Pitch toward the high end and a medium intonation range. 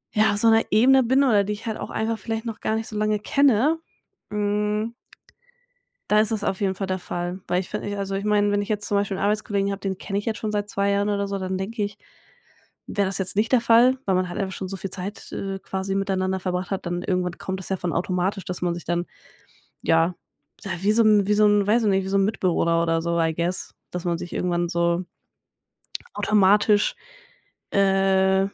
No: high, 200 Hz; narrow, 2.1 semitones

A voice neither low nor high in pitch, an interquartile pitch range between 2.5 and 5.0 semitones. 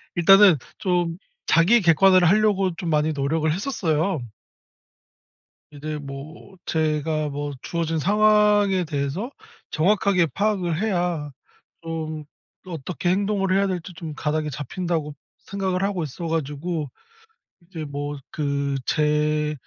Yes: medium, 165 Hz; average, 3.9 semitones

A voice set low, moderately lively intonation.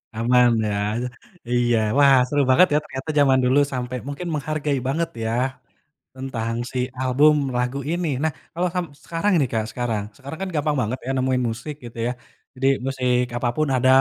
Yes: low, 130 Hz; average, 3.3 semitones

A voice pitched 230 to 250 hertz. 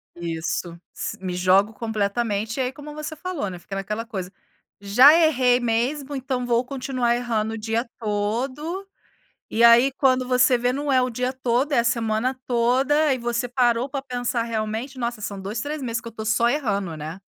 Yes: high, 240 Hz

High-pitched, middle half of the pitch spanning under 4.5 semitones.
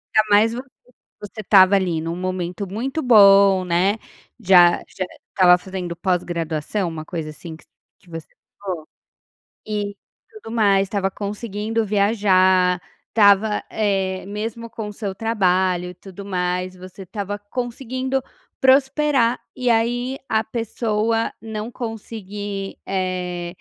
Yes: high, 200 Hz; average, 3.4 semitones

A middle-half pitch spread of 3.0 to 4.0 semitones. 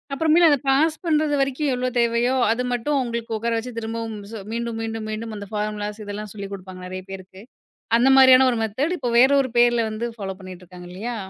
Yes: average, 3.6 semitones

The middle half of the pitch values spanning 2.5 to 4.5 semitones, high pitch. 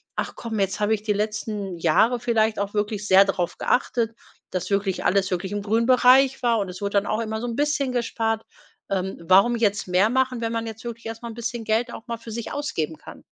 Yes: average, 2.8 semitones; high, 220 Hz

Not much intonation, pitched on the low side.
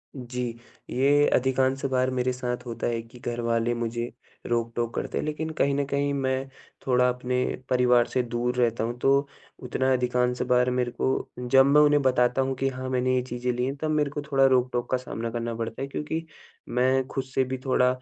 Yes: narrow, 1.6 semitones; low, 125 Hz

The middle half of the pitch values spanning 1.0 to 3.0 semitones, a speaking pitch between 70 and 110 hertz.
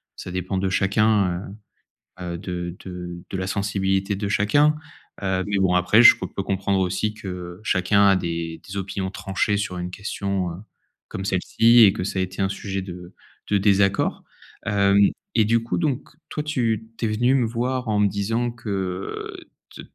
Yes: narrow, 2.4 semitones; low, 100 Hz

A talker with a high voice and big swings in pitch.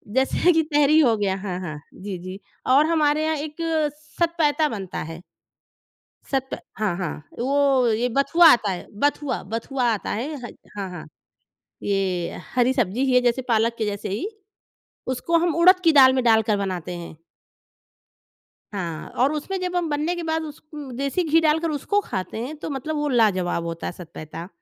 Yes: very high, 255 Hz; wide, 7.5 semitones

